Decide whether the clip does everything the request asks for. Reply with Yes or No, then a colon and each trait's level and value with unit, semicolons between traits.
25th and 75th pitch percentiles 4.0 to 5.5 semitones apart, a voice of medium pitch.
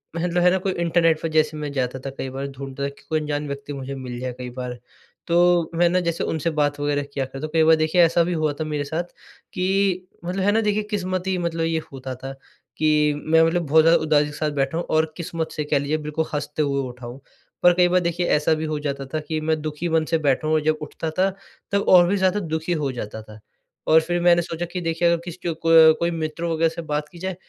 No: average, 3.1 semitones; medium, 160 Hz